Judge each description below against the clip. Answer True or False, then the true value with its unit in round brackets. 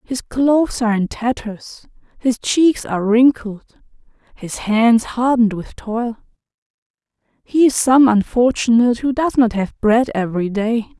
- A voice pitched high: True (235 Hz)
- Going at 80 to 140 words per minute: True (135 wpm)